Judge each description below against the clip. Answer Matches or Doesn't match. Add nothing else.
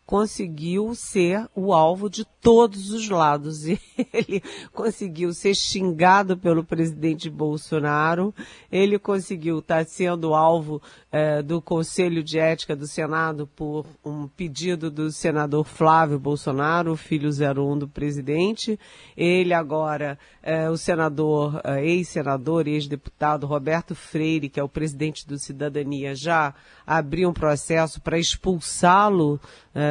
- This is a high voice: Doesn't match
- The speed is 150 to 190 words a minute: Doesn't match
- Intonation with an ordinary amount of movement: Matches